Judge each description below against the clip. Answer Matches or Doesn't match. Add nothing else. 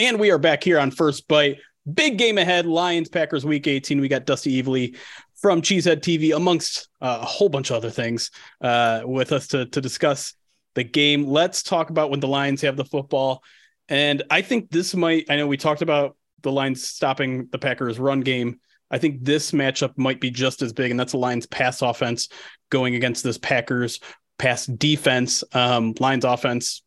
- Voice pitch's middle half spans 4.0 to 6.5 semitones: Doesn't match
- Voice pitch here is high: Doesn't match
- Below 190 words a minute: Doesn't match